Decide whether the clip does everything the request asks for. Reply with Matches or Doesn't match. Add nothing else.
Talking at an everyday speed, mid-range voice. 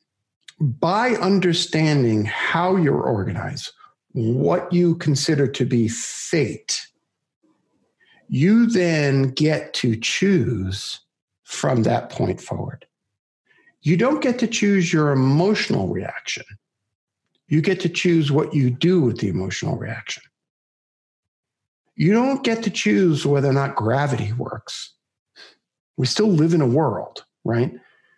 Doesn't match